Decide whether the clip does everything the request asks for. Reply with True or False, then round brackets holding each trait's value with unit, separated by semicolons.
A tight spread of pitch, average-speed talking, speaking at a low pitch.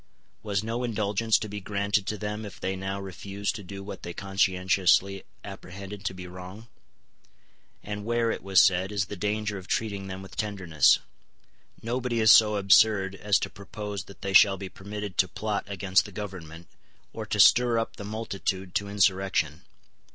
True (1.7 semitones; 175 wpm; 100 Hz)